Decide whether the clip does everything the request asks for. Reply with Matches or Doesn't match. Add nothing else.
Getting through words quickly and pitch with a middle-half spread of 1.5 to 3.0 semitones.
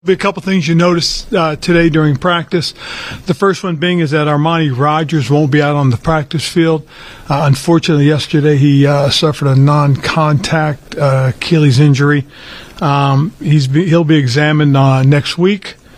Doesn't match